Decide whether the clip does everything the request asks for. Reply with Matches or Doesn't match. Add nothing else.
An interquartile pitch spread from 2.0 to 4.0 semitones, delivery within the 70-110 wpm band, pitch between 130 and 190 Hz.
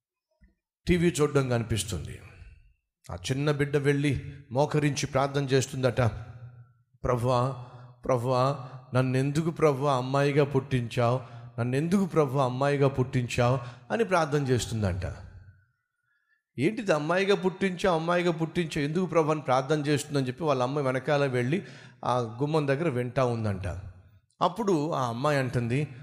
Matches